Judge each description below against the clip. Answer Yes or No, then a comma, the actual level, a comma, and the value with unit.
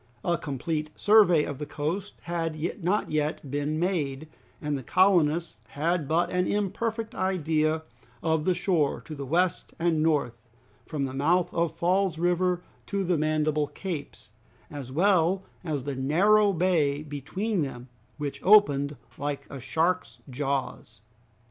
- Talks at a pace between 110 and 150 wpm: Yes, average, 145 wpm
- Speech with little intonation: No, average, 3.9 semitones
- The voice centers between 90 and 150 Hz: No, medium, 160 Hz